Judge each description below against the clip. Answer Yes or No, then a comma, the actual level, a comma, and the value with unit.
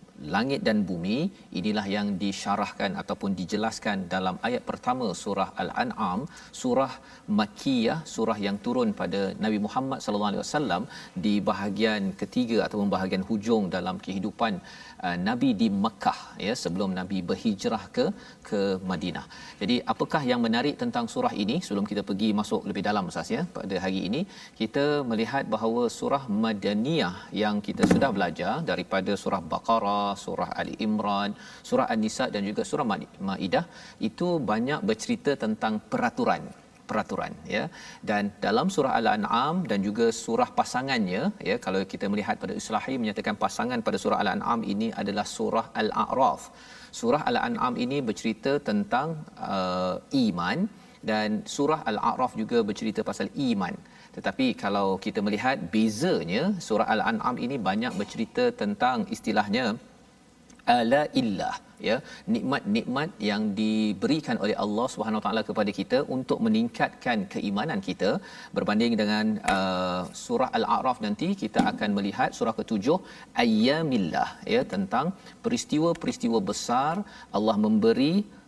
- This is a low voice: No, high, 205 Hz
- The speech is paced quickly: Yes, fast, 130 wpm